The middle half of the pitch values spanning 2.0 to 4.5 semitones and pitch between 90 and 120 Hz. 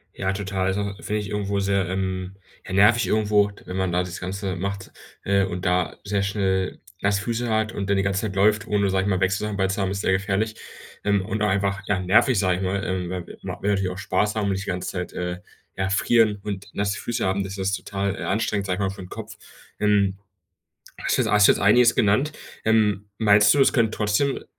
No: narrow, 1.5 semitones; low, 100 Hz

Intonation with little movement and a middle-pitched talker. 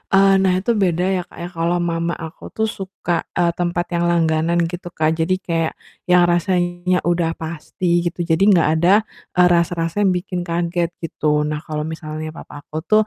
Yes: narrow, 1.7 semitones; medium, 170 Hz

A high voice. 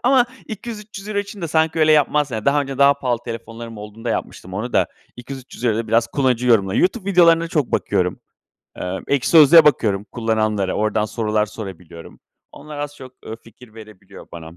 No: low, 125 Hz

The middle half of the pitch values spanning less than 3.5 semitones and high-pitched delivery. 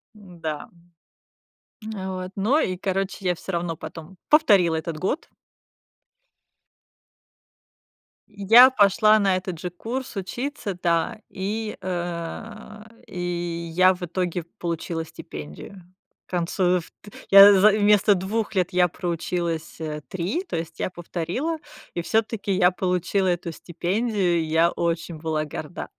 No: average, 3.1 semitones; medium, 180 Hz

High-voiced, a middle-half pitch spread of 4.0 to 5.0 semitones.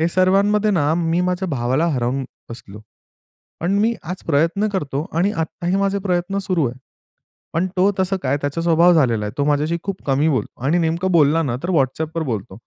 No: medium, 165 Hz; average, 4.6 semitones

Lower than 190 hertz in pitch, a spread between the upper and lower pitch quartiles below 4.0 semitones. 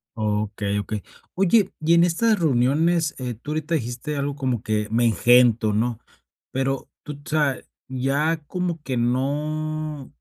No: low, 135 Hz; average, 4.5 semitones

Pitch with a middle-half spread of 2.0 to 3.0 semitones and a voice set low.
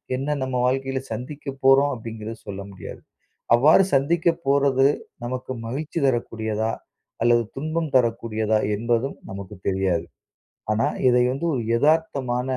No: average, 3.7 semitones; low, 125 Hz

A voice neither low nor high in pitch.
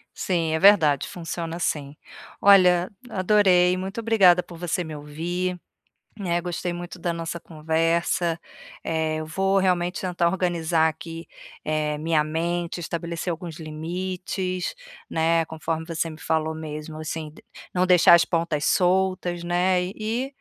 Yes: medium, 170 Hz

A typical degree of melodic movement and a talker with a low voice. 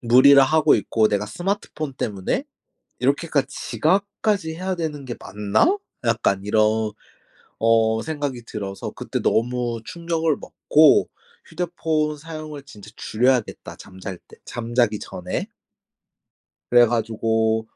No: wide, 6.0 semitones; low, 125 Hz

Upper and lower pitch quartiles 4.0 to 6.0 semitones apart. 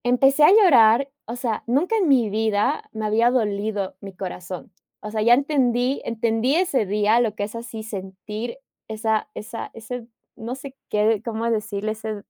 No: average, 2.8 semitones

